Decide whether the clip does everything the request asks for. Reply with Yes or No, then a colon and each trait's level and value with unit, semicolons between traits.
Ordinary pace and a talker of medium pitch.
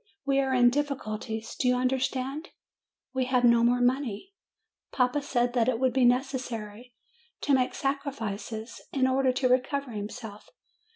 No: average, 155 wpm; very high, 250 Hz